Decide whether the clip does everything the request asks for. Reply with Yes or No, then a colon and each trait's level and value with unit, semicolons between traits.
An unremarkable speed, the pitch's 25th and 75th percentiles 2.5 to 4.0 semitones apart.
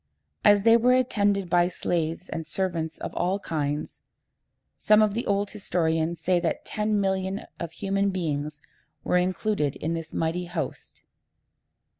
Yes: average, 145 wpm; average, 3.7 semitones